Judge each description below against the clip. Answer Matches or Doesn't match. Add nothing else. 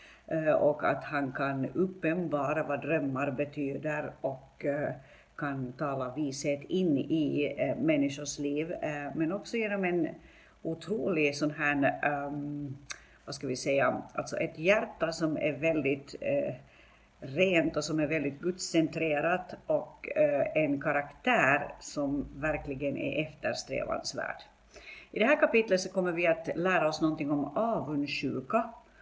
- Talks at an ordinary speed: Doesn't match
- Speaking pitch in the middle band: Matches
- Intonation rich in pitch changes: Doesn't match